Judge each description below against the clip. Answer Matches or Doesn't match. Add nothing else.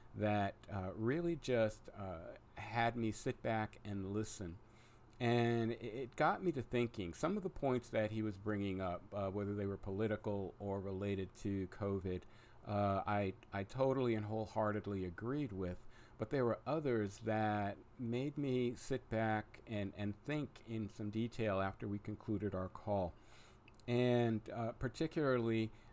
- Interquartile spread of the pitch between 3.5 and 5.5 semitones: Doesn't match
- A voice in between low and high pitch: Doesn't match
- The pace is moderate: Matches